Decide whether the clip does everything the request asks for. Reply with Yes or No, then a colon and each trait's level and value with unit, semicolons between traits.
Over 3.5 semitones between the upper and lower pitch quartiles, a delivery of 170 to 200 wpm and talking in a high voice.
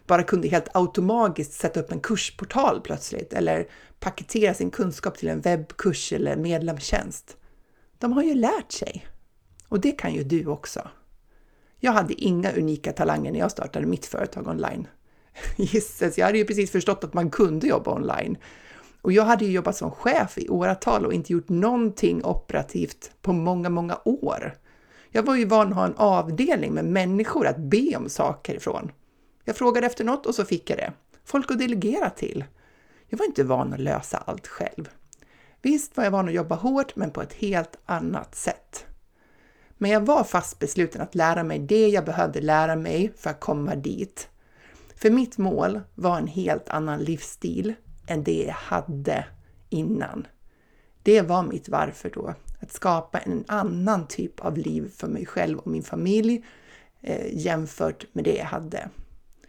Yes: average, 4.4 semitones; average, 175 wpm; high, 195 Hz